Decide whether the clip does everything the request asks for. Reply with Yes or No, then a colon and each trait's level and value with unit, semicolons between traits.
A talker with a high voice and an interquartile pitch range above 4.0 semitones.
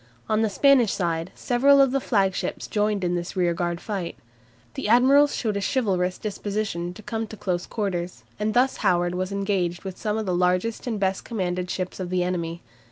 No: high, 195 Hz; average, 3.5 semitones